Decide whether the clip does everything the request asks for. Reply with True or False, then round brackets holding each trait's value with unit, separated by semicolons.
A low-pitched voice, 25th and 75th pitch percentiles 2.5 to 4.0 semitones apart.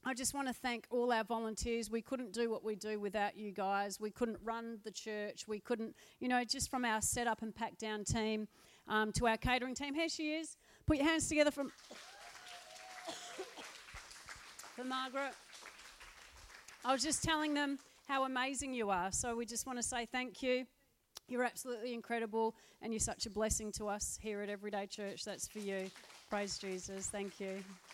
False (230 Hz; 3.3 semitones)